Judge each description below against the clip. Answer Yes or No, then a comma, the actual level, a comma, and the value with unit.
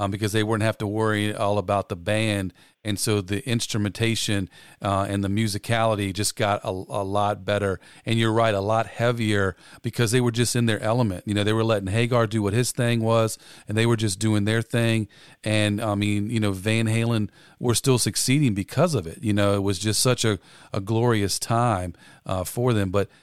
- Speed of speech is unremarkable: No, fast, 215 wpm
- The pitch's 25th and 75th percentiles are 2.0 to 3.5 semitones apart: Yes, narrow, 2.4 semitones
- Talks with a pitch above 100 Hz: Yes, low, 110 Hz